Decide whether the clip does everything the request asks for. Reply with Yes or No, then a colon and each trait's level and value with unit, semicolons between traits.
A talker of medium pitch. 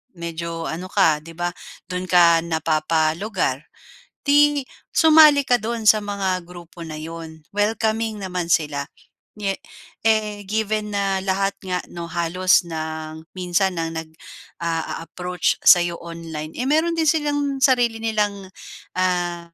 Yes: medium, 180 Hz